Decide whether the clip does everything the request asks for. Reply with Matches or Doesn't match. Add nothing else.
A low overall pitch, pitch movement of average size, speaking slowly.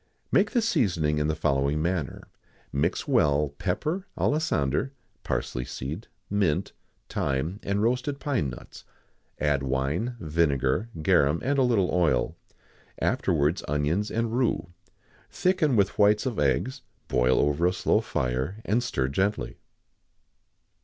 Doesn't match